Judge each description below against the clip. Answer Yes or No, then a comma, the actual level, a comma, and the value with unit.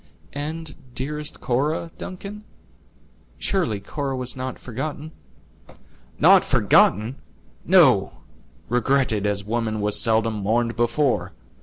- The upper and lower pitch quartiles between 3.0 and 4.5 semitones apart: No, average, 5.2 semitones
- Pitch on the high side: No, low, 125 Hz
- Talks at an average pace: No, slow, 100 wpm